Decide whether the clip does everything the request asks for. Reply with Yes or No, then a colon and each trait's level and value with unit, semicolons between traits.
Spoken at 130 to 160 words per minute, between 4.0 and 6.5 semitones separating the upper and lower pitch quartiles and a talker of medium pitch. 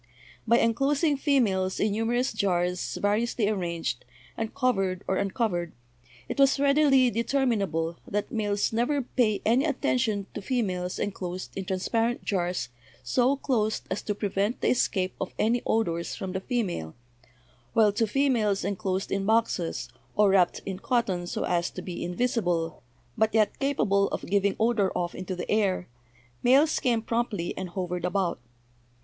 No: average, 155 wpm; average, 4.4 semitones; high, 205 Hz